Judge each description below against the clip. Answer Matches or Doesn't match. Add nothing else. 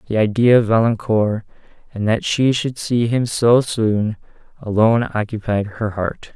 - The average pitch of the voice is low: Matches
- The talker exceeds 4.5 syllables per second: Doesn't match